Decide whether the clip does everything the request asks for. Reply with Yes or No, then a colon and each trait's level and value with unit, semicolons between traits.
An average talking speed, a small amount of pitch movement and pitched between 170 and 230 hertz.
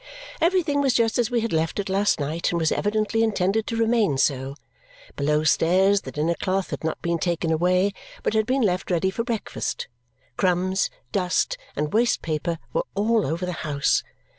No: average, 185 wpm; wide, 5.4 semitones; high, 190 Hz